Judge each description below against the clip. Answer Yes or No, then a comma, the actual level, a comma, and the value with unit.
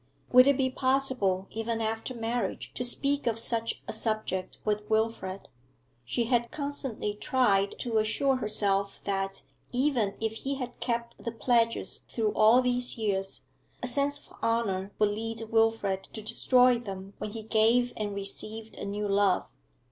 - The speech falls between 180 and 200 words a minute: No, average, 155 wpm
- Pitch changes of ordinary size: Yes, average, 3.1 semitones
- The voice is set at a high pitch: Yes, high, 225 Hz